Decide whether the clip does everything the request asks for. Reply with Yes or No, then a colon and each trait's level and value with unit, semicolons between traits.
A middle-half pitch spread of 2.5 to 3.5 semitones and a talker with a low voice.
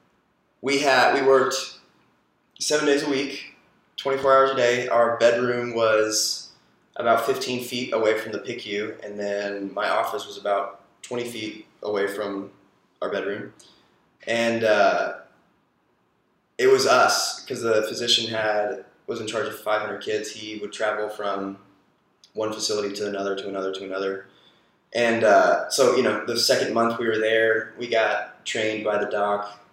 Yes: average, 2.8 semitones; low, 110 Hz